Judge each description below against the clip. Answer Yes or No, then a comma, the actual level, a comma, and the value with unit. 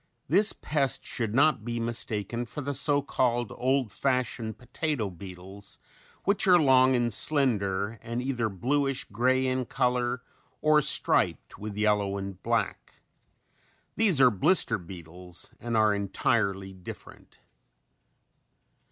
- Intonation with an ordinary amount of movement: Yes, average, 4.8 semitones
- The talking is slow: Yes, slow, 125 wpm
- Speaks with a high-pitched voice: No, low, 120 Hz